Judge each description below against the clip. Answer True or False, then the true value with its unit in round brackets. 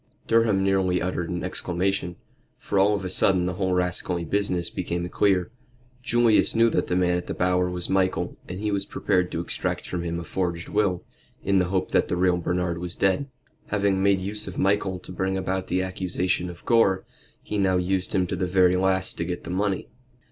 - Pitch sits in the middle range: False (95 Hz)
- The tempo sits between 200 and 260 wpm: True (205 wpm)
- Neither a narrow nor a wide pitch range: False (1.5 semitones)